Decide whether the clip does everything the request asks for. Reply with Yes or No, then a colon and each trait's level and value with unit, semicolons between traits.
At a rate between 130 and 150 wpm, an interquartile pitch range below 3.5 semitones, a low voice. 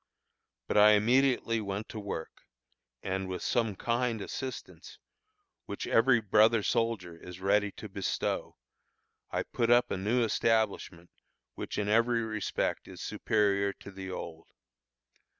Yes: slow, 135 wpm; average, 2.9 semitones; low, 105 Hz